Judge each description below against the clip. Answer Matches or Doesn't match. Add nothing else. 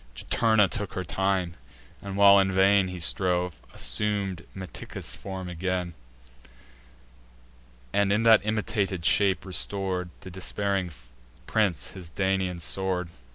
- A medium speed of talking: Doesn't match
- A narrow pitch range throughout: Matches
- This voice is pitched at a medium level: Doesn't match